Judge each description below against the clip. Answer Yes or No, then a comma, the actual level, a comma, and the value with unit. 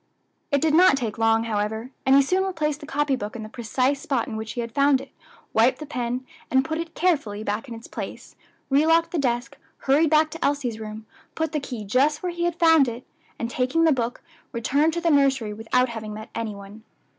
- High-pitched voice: Yes, very high, 265 Hz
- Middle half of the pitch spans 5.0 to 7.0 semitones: Yes, average, 5.3 semitones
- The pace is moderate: No, fast, 225 wpm